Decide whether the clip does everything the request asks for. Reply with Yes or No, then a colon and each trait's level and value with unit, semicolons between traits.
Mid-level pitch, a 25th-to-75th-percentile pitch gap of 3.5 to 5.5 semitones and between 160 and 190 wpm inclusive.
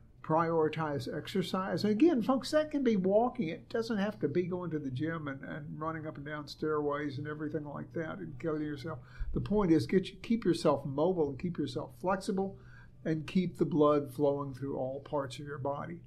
No: medium, 160 Hz; average, 4.4 semitones; average, 200 wpm